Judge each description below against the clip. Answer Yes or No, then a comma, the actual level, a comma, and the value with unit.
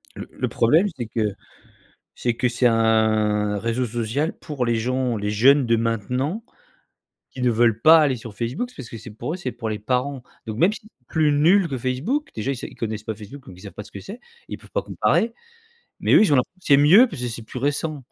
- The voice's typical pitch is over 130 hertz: No, low, 125 Hz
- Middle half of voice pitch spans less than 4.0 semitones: No, average, 4.6 semitones